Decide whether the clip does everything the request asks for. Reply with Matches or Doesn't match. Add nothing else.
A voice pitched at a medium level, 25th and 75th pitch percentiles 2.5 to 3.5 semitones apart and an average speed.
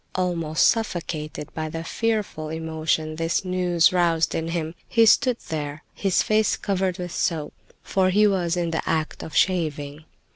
Matches